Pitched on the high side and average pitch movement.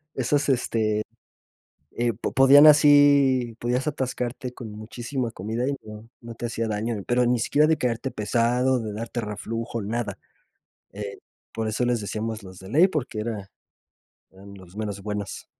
No: low, 115 Hz; average, 3.1 semitones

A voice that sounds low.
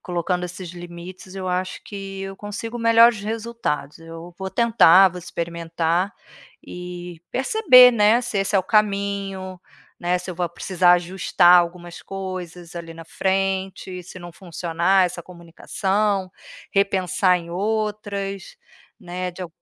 No: medium, 185 Hz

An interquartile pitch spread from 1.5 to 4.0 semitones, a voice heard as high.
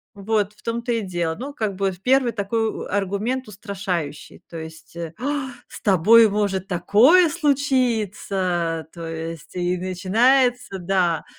No: average, 4.9 semitones; high, 200 Hz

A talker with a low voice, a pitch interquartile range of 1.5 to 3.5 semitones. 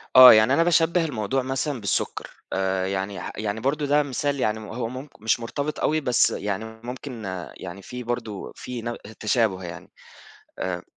No: low, 120 Hz; average, 4.7 semitones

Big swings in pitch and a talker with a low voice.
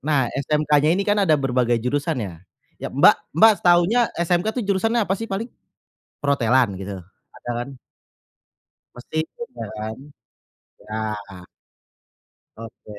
No: wide, 8.0 semitones; medium, 145 Hz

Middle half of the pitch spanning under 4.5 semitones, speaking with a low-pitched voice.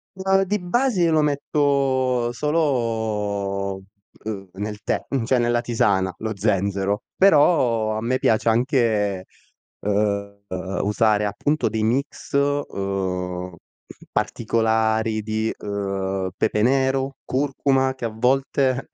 No: average, 4.9 semitones; low, 115 Hz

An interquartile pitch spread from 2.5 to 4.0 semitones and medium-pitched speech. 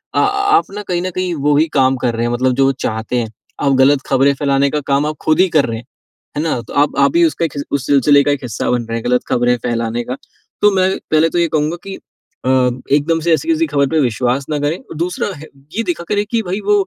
No: average, 5.0 semitones; medium, 145 Hz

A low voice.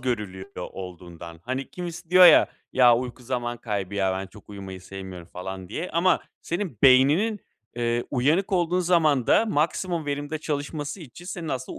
Yes: low, 130 Hz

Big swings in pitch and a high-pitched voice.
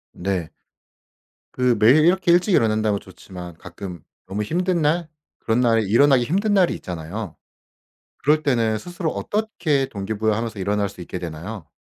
No: wide, 7.9 semitones; low, 110 Hz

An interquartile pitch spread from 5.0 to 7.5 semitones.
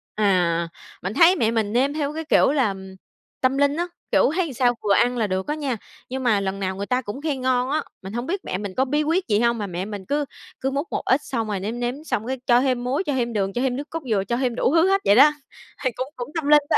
Yes: average, 5.3 semitones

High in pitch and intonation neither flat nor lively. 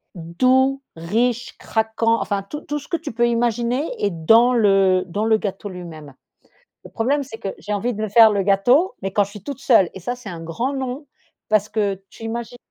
Yes: high, 220 Hz; average, 3.9 semitones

